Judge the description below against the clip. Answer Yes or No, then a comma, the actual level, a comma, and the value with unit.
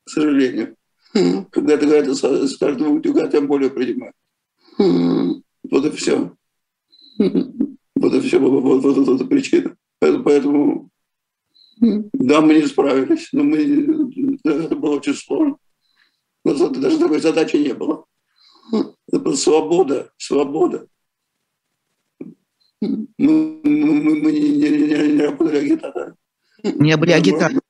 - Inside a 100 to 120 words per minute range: Yes, average, 115 wpm